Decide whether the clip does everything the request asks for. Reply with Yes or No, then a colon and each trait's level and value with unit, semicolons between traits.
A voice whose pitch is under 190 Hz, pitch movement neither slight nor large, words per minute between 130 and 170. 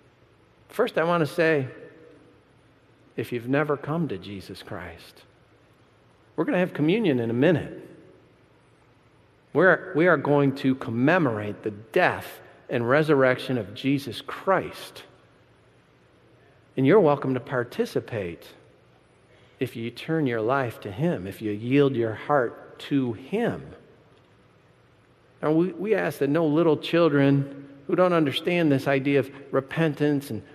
Yes: medium, 140 Hz; average, 4.4 semitones; slow, 135 wpm